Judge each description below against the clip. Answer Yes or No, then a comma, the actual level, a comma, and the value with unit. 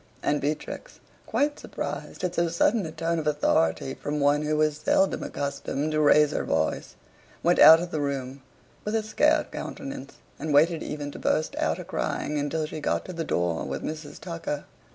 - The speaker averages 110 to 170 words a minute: No, average, 190 wpm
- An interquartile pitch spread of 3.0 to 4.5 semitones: No, narrow, 2.6 semitones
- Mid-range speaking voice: Yes, medium, 150 Hz